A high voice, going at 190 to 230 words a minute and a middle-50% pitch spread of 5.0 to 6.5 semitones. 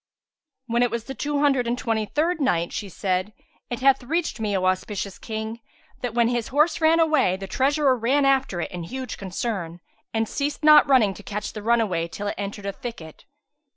Yes: high, 235 Hz; average, 200 wpm; wide, 5.4 semitones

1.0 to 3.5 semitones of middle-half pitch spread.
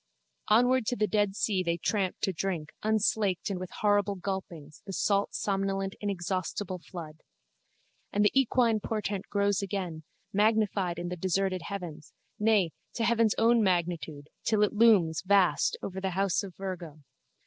Yes: average, 2.7 semitones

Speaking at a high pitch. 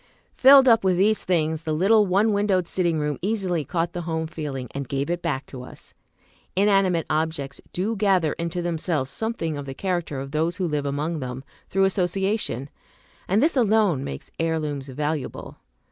No: medium, 170 Hz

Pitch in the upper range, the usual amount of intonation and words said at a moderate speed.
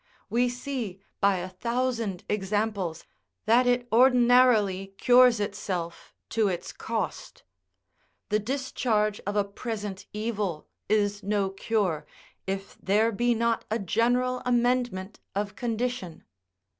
No: high, 215 Hz; average, 3.6 semitones; slow, 115 wpm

